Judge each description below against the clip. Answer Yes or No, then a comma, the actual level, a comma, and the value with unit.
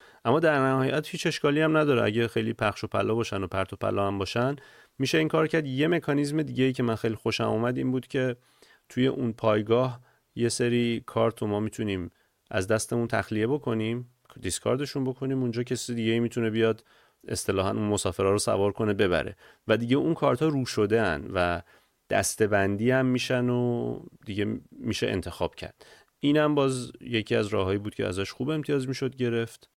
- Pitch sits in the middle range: No, low, 120 Hz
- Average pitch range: Yes, average, 3.4 semitones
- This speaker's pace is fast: Yes, fast, 185 wpm